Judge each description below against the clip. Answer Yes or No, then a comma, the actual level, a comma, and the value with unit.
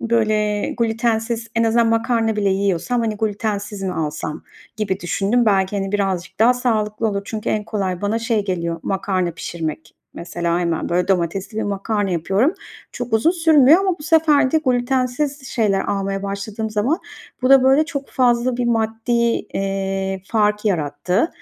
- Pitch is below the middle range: No, high, 215 Hz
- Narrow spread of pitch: No, average, 3.6 semitones